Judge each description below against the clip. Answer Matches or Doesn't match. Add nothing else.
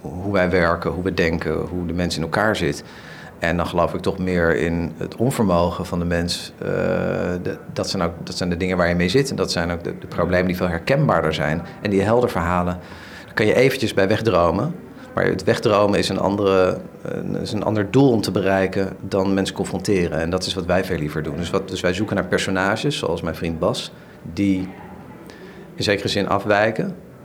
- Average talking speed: Doesn't match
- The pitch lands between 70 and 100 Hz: Matches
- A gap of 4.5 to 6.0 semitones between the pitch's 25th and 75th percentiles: Doesn't match